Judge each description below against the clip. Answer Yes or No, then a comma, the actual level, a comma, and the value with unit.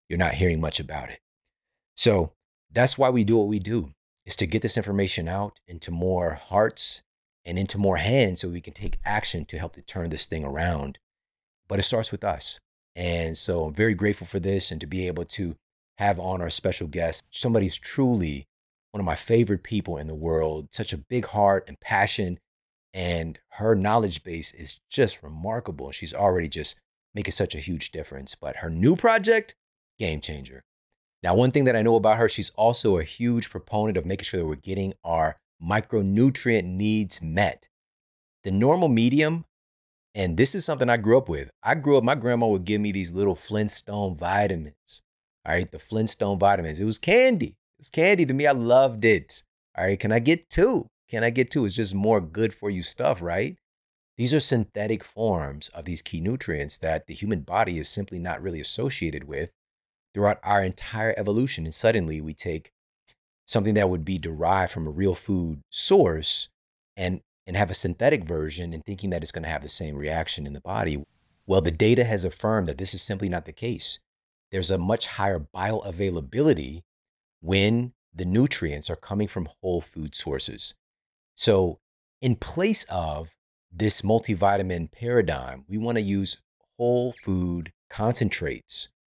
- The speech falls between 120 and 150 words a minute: No, average, 185 wpm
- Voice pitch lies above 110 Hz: No, very low, 95 Hz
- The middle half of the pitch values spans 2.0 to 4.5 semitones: No, average, 4.9 semitones